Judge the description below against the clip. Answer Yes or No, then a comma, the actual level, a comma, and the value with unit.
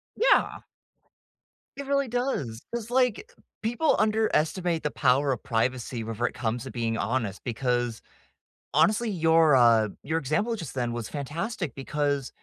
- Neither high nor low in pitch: Yes, medium, 145 Hz